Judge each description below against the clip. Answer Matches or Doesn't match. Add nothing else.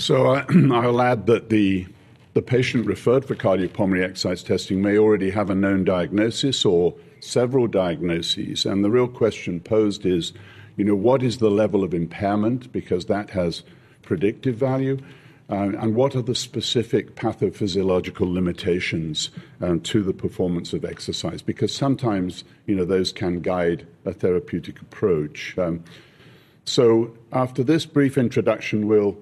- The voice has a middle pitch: Doesn't match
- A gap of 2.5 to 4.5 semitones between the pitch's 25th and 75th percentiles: Doesn't match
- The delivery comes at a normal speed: Matches